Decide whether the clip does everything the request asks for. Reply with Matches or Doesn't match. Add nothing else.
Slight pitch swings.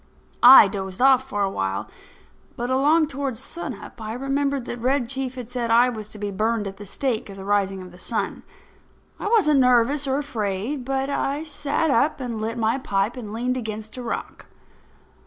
Doesn't match